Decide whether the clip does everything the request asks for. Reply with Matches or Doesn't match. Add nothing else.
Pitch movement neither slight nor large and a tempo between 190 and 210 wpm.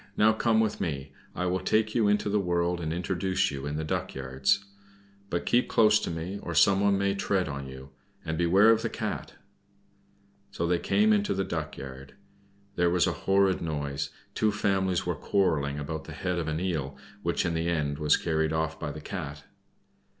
Matches